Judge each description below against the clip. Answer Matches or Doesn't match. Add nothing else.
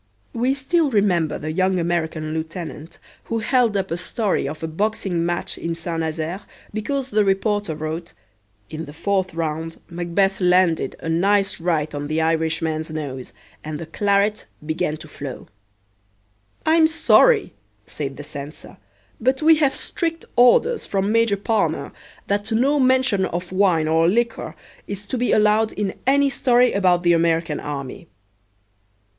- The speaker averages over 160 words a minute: Doesn't match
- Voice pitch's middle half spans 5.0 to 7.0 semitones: Matches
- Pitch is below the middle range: Doesn't match